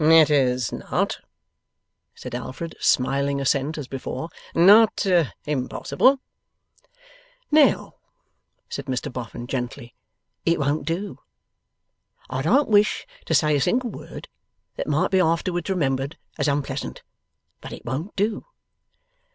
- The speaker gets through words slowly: Yes, slow, 120 wpm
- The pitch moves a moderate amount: No, wide, 5.7 semitones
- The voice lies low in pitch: No, medium, 150 Hz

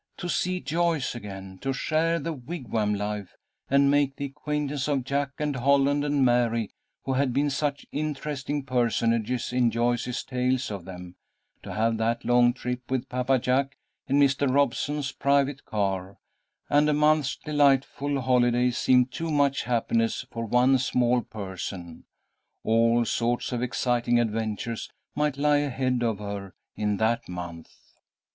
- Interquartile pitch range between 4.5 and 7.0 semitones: No, average, 3.5 semitones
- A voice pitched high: No, low, 125 Hz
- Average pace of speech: Yes, average, 145 wpm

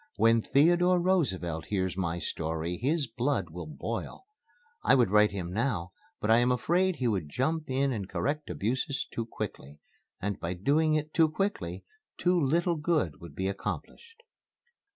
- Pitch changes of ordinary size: No, wide, 9.0 semitones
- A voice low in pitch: Yes, low, 115 Hz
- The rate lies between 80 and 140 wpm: No, average, 165 wpm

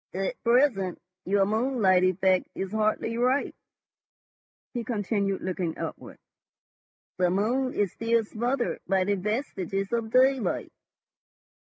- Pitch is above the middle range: Yes, high, 210 Hz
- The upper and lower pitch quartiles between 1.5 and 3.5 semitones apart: No, average, 3.9 semitones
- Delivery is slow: Yes, slow, 110 wpm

